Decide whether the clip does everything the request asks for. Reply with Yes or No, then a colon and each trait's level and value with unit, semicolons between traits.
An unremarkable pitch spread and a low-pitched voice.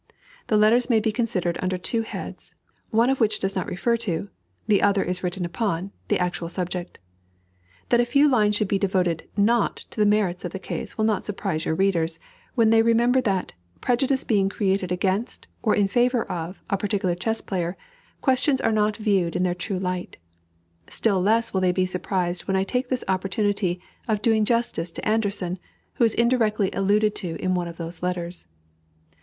No: average, 3.7 semitones; high, 200 Hz